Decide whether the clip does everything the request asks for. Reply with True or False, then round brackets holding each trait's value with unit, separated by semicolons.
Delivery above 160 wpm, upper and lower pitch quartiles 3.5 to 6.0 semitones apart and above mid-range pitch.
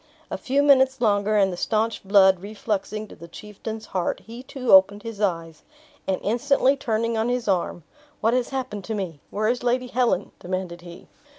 True (185 wpm; 4.2 semitones; 215 Hz)